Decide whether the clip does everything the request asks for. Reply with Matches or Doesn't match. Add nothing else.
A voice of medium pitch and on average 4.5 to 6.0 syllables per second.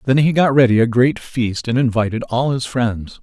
Doesn't match